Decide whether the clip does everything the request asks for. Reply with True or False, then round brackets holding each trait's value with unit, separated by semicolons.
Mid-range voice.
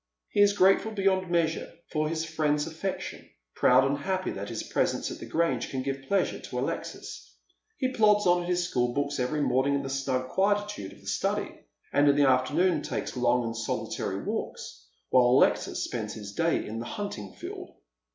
True (145 Hz)